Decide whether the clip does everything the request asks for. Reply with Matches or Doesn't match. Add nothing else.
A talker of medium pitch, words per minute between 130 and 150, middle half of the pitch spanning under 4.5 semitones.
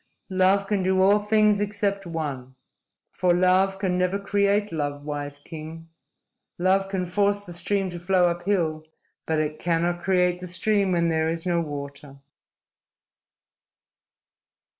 Matches